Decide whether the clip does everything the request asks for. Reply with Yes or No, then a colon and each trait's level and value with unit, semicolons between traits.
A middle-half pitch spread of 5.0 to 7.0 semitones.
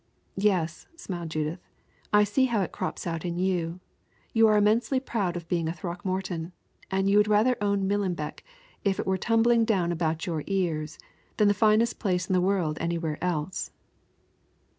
No: average, 3.6 semitones